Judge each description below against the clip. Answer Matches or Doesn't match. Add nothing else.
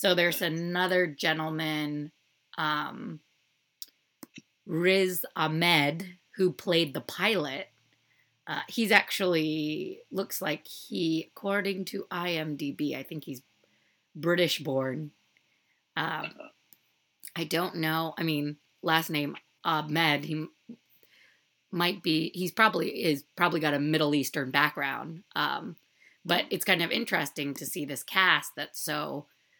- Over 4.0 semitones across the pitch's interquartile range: Doesn't match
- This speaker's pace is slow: Matches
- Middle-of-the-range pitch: Matches